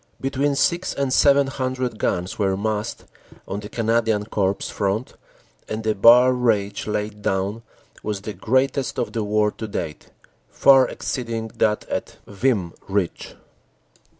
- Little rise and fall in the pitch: No, average, 3.8 semitones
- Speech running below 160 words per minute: Yes, average, 145 wpm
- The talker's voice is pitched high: No, low, 110 Hz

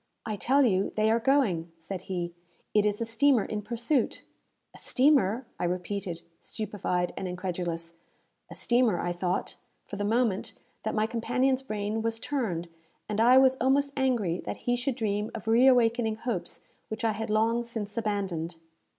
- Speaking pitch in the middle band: No, high, 220 Hz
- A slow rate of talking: No, average, 165 wpm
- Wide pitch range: No, average, 4.2 semitones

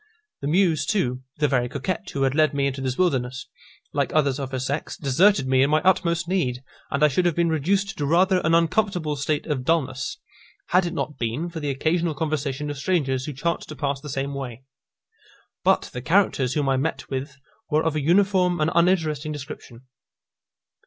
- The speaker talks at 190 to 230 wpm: Yes, average, 195 wpm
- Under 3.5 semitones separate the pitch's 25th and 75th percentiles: No, average, 3.9 semitones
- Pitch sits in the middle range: Yes, medium, 150 Hz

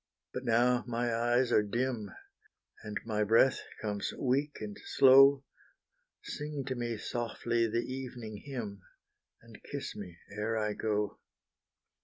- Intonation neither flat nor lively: Yes, average, 3.3 semitones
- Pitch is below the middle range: Yes, low, 120 Hz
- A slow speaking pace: Yes, slow, 130 wpm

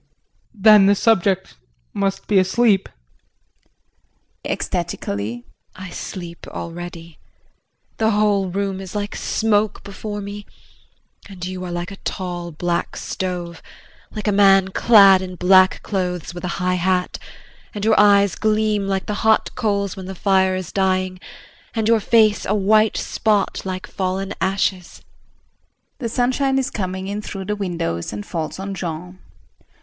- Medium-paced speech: Yes, average, 145 wpm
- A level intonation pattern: Yes, narrow, 2.3 semitones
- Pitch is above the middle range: Yes, high, 195 Hz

